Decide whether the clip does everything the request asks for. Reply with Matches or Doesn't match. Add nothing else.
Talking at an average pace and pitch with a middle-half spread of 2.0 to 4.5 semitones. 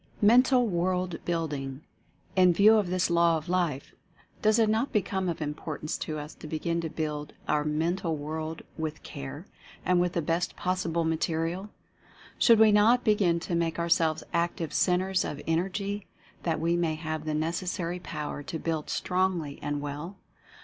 Matches